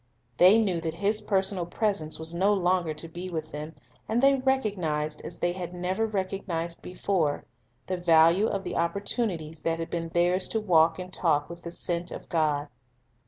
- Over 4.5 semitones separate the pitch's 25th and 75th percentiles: No, average, 3.1 semitones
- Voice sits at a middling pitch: Yes, medium, 175 Hz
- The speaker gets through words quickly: No, average, 185 wpm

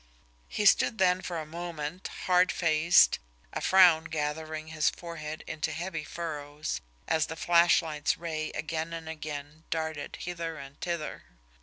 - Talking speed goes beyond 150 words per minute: No, slow, 135 wpm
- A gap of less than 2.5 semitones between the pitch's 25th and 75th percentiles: Yes, narrow, 1.8 semitones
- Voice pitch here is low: No, medium, 160 Hz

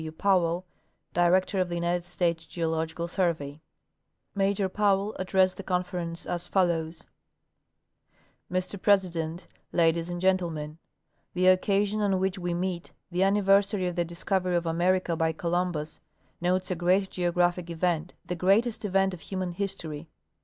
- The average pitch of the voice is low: No, medium, 180 Hz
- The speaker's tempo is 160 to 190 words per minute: No, average, 140 wpm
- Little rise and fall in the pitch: Yes, narrow, 2.0 semitones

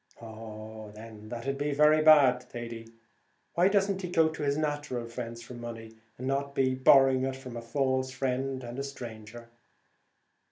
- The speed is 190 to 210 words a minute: No, average, 170 wpm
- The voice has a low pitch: Yes, low, 130 Hz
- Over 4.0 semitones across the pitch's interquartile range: No, average, 3.2 semitones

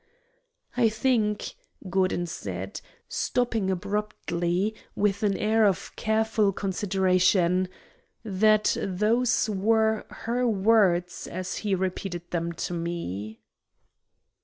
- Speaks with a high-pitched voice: Yes, high, 195 Hz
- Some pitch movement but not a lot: Yes, average, 3.5 semitones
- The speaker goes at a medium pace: No, slow, 95 wpm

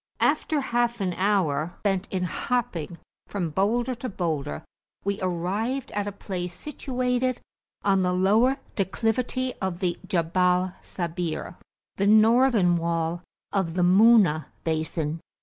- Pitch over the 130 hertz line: Yes, high, 190 Hz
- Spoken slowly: Yes, slow, 125 wpm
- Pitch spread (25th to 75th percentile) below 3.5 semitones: No, average, 4.8 semitones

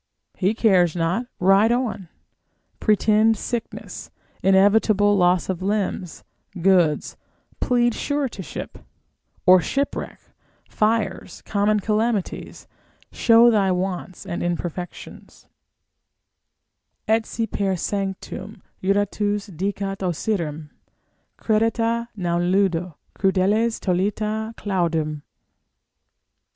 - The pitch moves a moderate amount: Yes, average, 3.3 semitones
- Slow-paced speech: Yes, slow, 85 wpm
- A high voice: Yes, high, 200 Hz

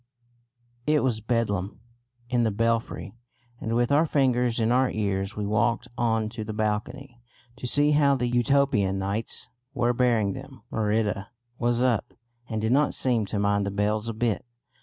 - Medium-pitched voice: No, low, 115 Hz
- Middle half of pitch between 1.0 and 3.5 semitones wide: Yes, average, 2.8 semitones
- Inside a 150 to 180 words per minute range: Yes, average, 160 wpm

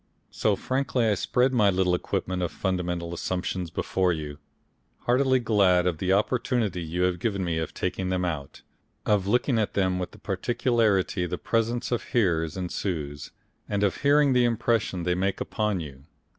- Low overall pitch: Yes, very low, 95 Hz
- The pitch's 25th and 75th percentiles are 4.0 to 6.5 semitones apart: Yes, average, 4.5 semitones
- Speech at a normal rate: Yes, average, 170 wpm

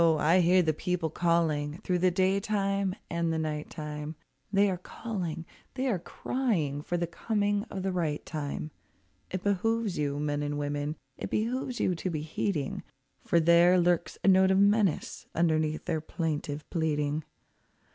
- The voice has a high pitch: No, medium, 170 Hz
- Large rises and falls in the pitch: No, average, 4.0 semitones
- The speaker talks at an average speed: Yes, average, 165 wpm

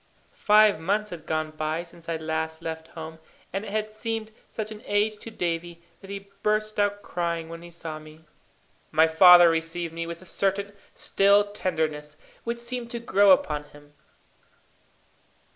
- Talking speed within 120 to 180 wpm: Yes, average, 165 wpm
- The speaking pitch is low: No, medium, 175 Hz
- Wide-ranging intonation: No, average, 4.4 semitones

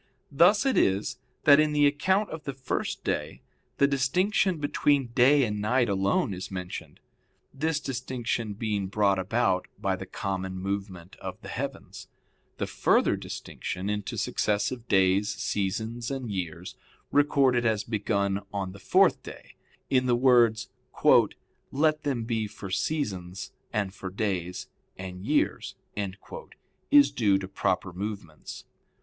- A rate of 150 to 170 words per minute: No, slow, 135 wpm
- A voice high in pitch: No, low, 110 Hz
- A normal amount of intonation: No, wide, 5.7 semitones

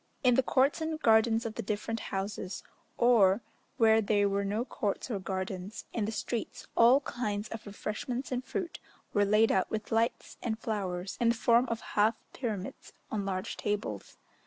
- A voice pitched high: Yes, high, 220 Hz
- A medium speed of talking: Yes, average, 175 wpm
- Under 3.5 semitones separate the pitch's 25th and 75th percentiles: Yes, average, 2.7 semitones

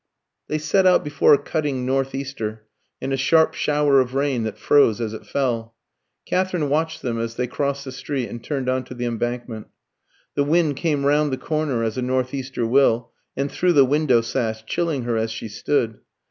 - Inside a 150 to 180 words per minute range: No, average, 200 wpm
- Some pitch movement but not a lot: Yes, average, 3.7 semitones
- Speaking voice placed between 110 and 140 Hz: Yes, low, 135 Hz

